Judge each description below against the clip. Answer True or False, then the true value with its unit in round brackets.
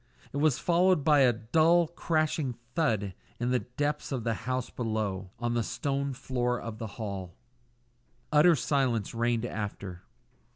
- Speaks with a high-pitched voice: False (125 Hz)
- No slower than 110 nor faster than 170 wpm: True (150 wpm)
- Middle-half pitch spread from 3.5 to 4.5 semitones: False (4.9 semitones)